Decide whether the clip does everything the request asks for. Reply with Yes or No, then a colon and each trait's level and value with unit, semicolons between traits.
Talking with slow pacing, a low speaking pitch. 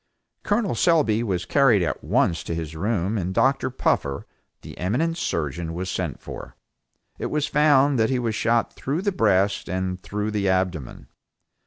No: average, 165 wpm; low, 105 Hz